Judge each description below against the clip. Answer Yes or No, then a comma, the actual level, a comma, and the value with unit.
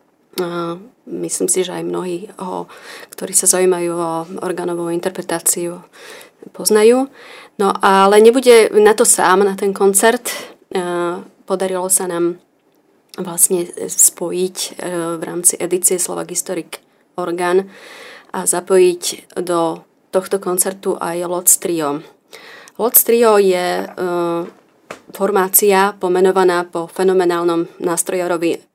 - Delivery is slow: Yes, slow, 100 wpm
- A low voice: No, medium, 185 Hz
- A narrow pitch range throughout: Yes, narrow, 2.2 semitones